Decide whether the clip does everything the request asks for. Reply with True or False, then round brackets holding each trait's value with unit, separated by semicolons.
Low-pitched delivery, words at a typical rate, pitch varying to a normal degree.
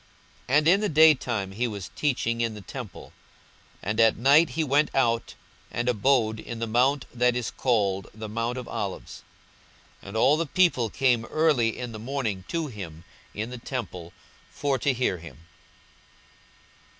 True (120 Hz; 175 wpm; 4.1 semitones)